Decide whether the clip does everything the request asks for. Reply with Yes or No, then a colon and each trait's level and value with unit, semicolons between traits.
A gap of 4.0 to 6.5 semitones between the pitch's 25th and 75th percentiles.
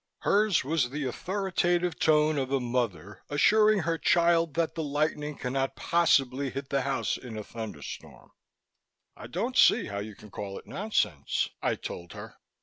Yes: wide, 5.4 semitones